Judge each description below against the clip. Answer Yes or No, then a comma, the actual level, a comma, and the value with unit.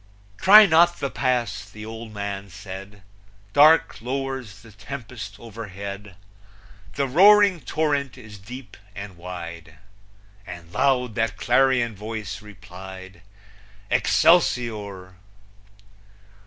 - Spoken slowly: Yes, slow, 100 wpm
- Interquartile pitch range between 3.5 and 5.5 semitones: Yes, average, 5.2 semitones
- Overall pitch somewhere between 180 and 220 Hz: No, low, 110 Hz